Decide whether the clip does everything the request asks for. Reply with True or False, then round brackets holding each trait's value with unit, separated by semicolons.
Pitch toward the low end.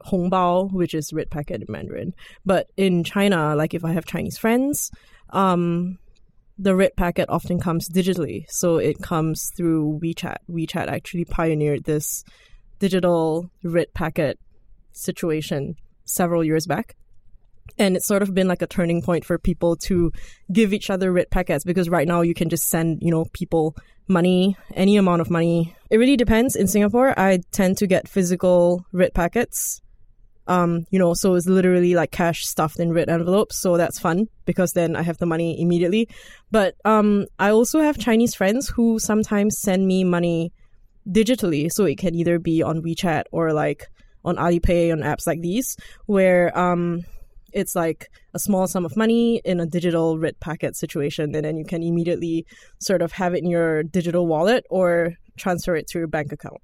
False (175 Hz)